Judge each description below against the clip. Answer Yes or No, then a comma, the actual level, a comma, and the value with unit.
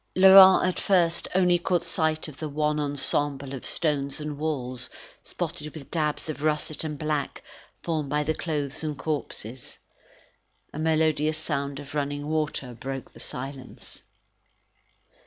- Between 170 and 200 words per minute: No, average, 140 wpm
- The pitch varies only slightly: Yes, narrow, 2.1 semitones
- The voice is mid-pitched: Yes, medium, 150 Hz